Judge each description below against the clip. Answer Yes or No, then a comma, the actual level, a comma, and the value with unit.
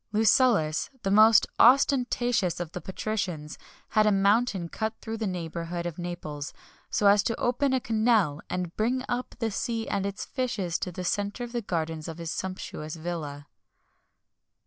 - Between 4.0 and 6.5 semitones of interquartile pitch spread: Yes, average, 4.9 semitones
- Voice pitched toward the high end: Yes, high, 200 Hz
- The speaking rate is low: No, average, 170 wpm